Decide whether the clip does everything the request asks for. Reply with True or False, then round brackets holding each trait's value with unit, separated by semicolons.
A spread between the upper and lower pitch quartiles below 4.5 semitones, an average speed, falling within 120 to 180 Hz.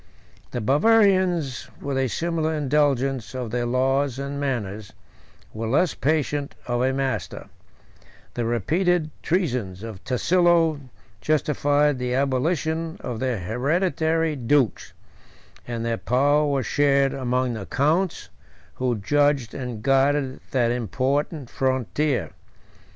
False (3.6 semitones; 115 wpm; 135 Hz)